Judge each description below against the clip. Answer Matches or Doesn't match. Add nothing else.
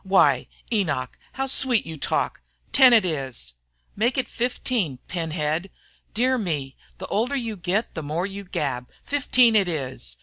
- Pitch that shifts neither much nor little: Doesn't match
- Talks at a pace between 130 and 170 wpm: Matches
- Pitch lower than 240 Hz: Matches